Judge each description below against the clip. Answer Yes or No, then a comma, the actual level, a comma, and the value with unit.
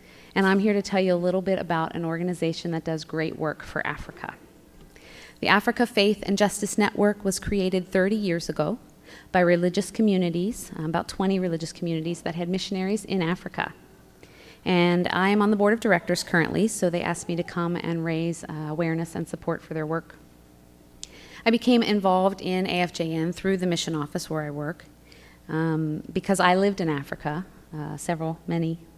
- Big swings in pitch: No, average, 2.9 semitones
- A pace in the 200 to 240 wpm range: No, average, 175 wpm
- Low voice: No, medium, 175 Hz